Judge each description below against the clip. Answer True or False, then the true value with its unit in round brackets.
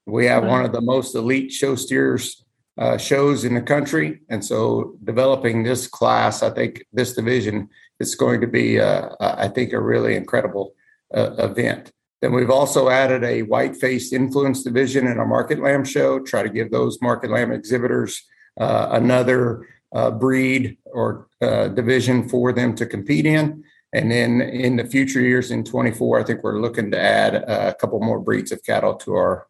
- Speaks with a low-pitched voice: True (125 Hz)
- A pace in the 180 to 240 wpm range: True (185 wpm)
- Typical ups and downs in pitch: False (1.7 semitones)